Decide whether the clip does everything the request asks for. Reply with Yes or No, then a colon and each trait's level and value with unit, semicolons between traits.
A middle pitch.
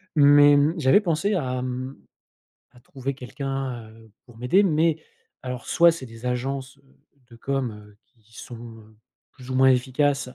No: low, 130 Hz